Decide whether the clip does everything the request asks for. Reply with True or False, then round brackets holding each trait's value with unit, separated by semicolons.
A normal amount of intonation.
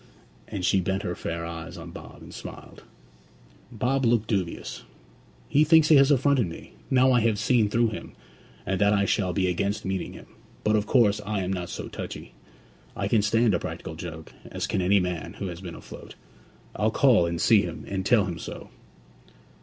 True (4.3 semitones)